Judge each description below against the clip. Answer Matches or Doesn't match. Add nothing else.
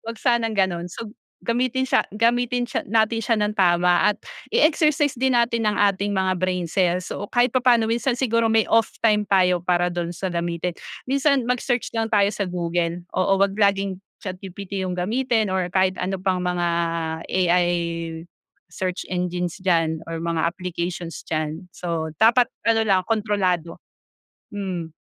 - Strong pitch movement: Doesn't match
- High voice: Matches